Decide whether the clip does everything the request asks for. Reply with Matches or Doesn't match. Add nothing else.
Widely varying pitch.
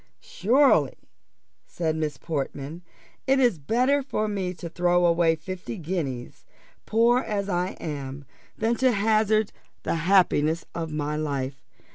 Matches